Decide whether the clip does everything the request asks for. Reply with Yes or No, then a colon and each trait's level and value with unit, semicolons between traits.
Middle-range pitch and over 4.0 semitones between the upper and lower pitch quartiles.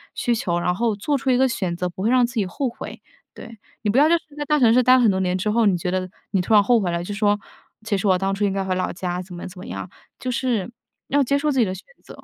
No: high, 210 Hz; average, 4.8 semitones